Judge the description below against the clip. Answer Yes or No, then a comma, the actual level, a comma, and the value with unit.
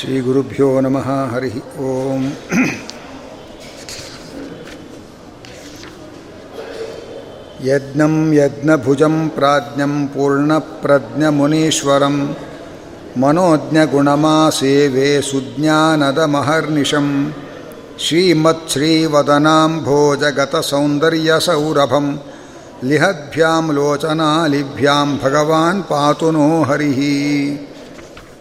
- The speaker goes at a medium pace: No, slow, 40 wpm